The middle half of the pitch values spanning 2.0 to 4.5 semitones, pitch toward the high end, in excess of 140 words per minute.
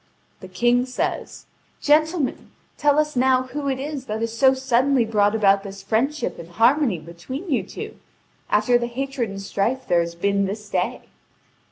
No: average, 5.3 semitones; high, 240 Hz; average, 170 wpm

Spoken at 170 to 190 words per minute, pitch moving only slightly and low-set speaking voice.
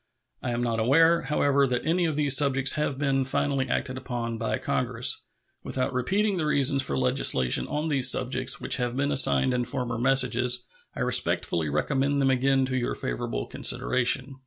Yes: average, 175 wpm; narrow, 2.2 semitones; low, 130 Hz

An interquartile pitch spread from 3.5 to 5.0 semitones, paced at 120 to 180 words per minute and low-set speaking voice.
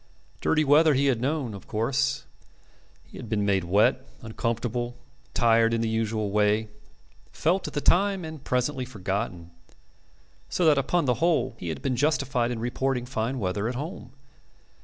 Yes: average, 4.2 semitones; average, 160 wpm; low, 120 Hz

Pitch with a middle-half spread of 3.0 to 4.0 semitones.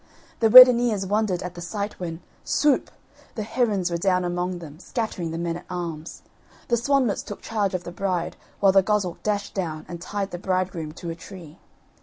Yes: average, 3.3 semitones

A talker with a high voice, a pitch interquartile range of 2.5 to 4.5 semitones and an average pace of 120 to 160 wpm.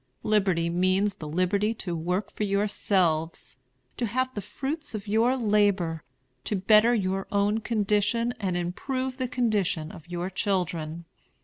Yes: high, 200 Hz; average, 3.8 semitones; average, 140 wpm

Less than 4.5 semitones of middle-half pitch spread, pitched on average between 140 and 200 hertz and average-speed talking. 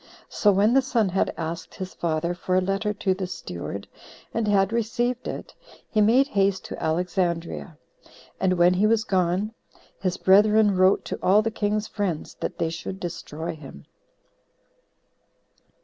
Yes: average, 3.4 semitones; high, 190 Hz; average, 155 wpm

